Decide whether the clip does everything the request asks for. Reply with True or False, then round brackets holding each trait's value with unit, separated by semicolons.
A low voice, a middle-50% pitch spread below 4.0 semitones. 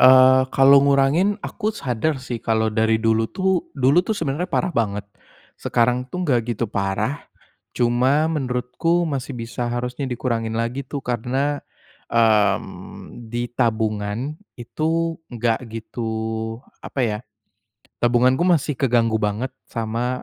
True (125 Hz; 3.6 semitones)